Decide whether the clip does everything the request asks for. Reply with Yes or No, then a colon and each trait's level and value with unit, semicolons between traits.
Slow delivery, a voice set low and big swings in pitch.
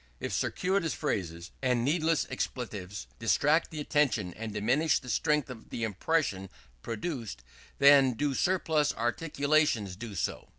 Yes: slow, 130 wpm; low, 130 Hz; wide, 5.9 semitones